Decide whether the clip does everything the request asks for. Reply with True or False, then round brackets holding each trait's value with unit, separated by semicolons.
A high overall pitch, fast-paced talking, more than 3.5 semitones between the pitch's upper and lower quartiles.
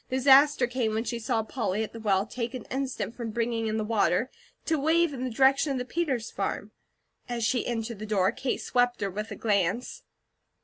False (235 Hz; 210 wpm; 3.1 semitones)